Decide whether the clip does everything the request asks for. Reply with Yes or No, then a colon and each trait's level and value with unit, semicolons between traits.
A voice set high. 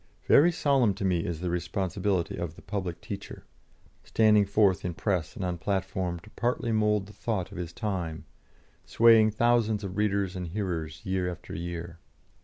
No: very low, 95 Hz